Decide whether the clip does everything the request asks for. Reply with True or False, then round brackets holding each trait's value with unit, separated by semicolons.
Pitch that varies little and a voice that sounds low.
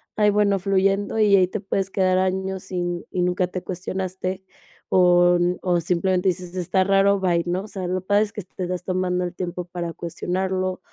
False (1.2 semitones; 185 Hz)